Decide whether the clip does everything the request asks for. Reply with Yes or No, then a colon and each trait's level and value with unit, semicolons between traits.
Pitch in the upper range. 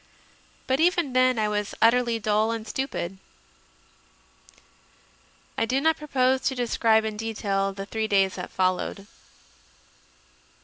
Yes: high, 225 Hz